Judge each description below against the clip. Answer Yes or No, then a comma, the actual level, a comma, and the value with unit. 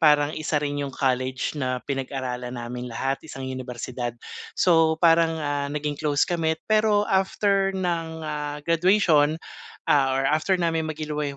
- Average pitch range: Yes, average, 3.6 semitones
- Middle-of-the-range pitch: Yes, medium, 150 Hz